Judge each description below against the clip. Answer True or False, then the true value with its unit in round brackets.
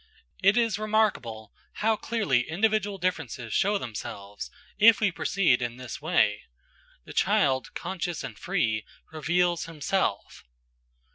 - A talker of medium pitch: True (175 Hz)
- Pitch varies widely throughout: True (8.9 semitones)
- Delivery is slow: True (120 wpm)